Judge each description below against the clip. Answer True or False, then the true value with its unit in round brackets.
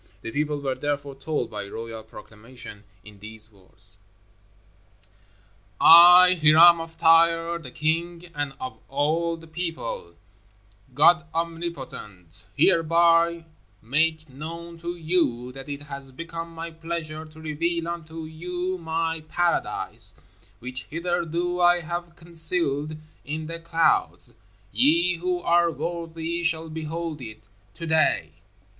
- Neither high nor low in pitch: True (160 Hz)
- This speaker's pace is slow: True (120 wpm)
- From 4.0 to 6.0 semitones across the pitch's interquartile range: False (3.3 semitones)